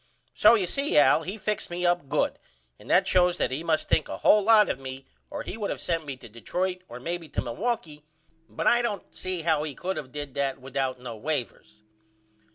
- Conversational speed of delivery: No, fast, 220 wpm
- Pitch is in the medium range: Yes, medium, 160 Hz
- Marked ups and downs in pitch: Yes, wide, 5.7 semitones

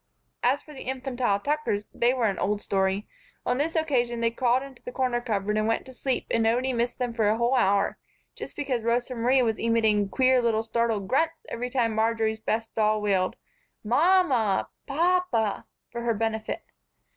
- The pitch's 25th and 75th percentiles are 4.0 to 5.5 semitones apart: No, average, 2.9 semitones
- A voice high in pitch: Yes, high, 235 Hz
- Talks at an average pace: Yes, average, 190 wpm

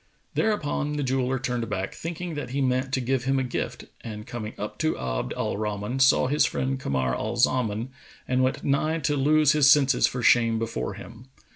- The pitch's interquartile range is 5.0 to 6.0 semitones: No, average, 3.6 semitones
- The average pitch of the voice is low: Yes, low, 130 Hz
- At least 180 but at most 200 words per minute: Yes, average, 195 wpm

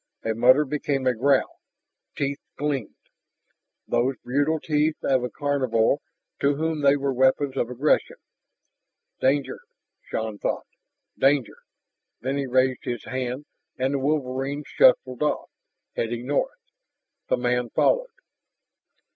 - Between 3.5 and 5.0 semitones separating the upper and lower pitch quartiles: No, narrow, 2.5 semitones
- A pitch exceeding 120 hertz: Yes, low, 135 Hz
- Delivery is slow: Yes, slow, 120 wpm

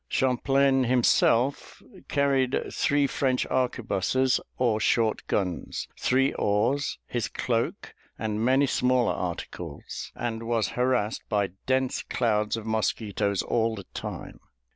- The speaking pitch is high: No, low, 120 Hz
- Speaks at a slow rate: Yes, slow, 115 wpm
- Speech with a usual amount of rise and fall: Yes, average, 3.1 semitones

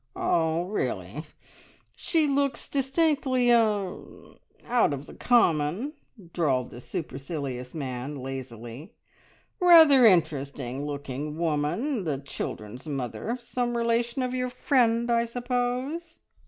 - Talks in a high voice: Yes, high, 195 Hz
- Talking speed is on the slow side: Yes, slow, 105 wpm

